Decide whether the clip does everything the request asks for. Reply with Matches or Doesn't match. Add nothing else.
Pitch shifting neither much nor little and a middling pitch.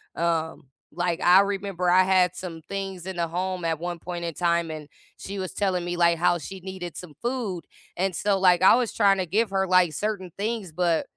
Doesn't match